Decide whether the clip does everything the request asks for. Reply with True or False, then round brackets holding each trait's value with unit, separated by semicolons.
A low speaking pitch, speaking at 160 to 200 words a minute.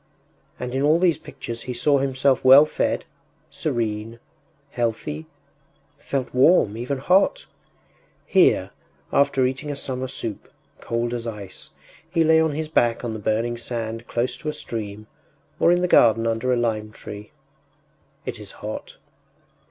False (120 Hz; 150 wpm)